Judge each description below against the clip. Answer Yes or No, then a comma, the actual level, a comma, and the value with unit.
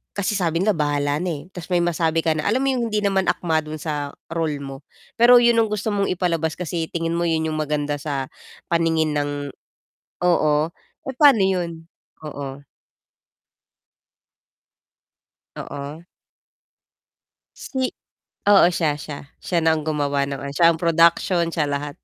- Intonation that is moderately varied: Yes, average, 3.4 semitones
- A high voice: No, medium, 165 Hz